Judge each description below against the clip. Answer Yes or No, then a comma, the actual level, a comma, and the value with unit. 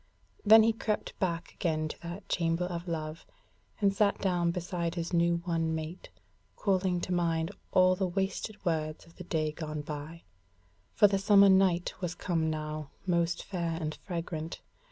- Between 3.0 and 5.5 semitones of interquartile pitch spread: No, narrow, 2.5 semitones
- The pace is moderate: Yes, average, 165 wpm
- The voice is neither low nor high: Yes, medium, 170 Hz